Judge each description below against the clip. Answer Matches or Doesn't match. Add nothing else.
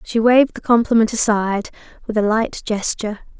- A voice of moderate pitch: Doesn't match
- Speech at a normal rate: Matches